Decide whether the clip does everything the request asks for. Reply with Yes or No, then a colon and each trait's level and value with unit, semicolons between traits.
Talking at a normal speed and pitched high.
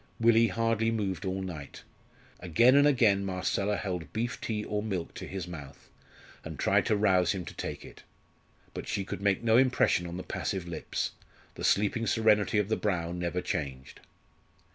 No: average, 175 wpm; low, 100 Hz